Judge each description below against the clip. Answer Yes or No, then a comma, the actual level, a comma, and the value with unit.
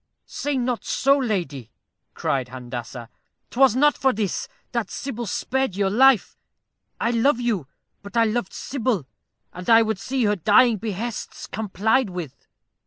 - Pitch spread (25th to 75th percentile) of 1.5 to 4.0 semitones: No, average, 5.2 semitones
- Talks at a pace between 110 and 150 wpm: Yes, average, 145 wpm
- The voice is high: Yes, high, 220 Hz